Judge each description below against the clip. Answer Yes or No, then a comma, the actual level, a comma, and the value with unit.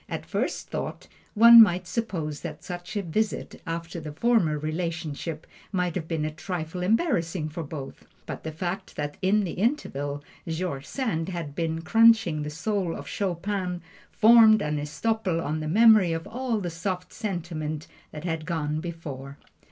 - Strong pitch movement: No, average, 4.2 semitones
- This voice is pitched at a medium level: Yes, medium, 170 Hz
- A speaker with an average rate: Yes, average, 160 wpm